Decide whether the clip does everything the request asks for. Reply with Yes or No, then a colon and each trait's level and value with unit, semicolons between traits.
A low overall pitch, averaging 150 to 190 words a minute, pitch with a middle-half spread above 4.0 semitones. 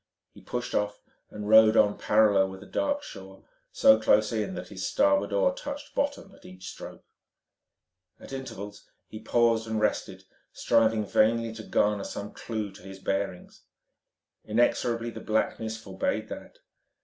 No: low, 110 Hz; average, 155 wpm; narrow, 2.4 semitones